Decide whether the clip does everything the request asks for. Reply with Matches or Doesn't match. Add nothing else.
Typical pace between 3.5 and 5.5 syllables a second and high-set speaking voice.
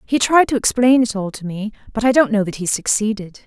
Doesn't match